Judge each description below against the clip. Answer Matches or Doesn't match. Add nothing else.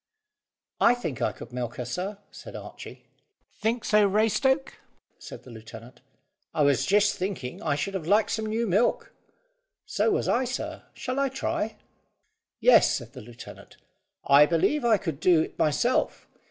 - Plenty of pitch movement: Matches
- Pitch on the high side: Matches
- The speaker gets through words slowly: Doesn't match